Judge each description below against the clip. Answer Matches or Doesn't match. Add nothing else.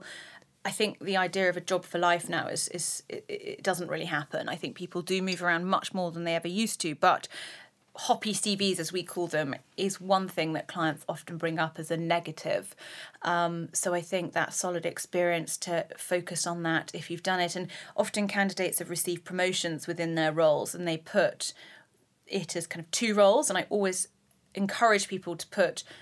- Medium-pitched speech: Matches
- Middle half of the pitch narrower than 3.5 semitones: Matches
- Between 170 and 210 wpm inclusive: Matches